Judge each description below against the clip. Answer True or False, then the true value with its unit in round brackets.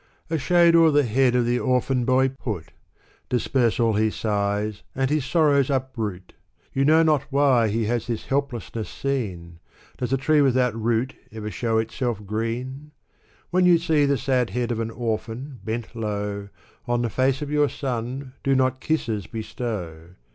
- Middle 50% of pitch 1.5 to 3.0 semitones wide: False (3.7 semitones)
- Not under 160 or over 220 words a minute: True (170 wpm)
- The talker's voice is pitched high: False (125 Hz)